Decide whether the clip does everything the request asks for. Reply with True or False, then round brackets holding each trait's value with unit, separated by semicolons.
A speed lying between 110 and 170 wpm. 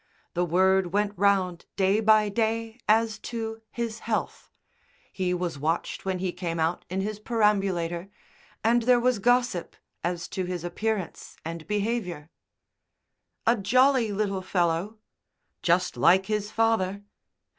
True (135 wpm)